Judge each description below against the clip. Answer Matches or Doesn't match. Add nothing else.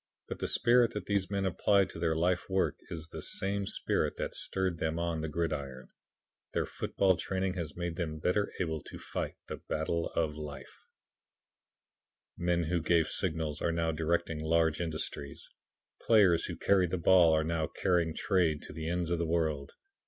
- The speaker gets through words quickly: Doesn't match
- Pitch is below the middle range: Matches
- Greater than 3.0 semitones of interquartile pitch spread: Doesn't match